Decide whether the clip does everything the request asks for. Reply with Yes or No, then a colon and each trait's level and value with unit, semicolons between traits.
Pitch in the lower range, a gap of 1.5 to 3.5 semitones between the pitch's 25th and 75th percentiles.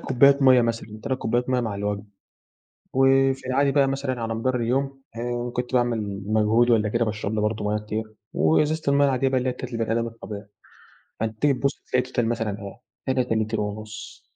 Yes: low, 120 Hz; average, 3.2 semitones